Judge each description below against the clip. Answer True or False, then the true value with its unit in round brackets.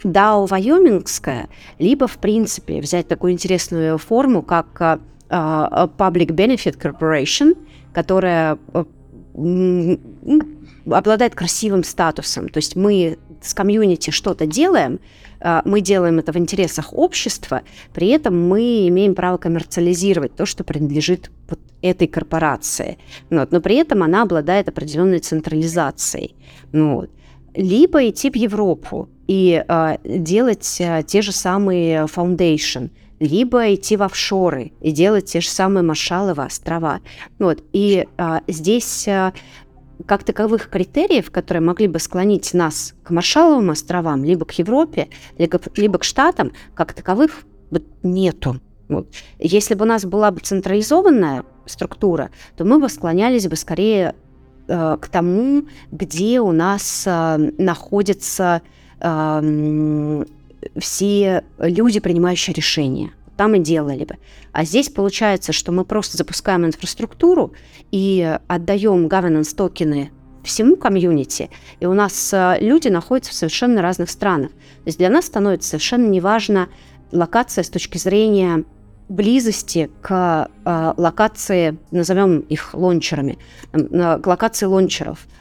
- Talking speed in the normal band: True (130 wpm)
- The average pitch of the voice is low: False (180 Hz)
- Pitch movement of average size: True (4.0 semitones)